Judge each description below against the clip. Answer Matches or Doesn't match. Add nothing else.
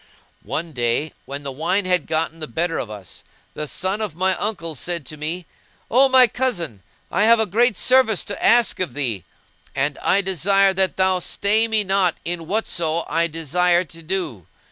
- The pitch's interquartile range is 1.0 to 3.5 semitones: Doesn't match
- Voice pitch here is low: Doesn't match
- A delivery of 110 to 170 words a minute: Doesn't match